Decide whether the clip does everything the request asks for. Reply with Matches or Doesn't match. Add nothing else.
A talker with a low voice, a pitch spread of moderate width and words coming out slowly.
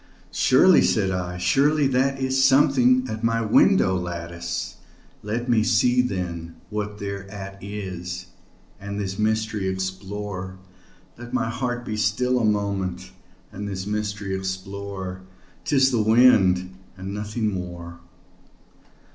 Matches